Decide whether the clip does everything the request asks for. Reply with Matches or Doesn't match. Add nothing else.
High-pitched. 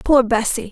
Matches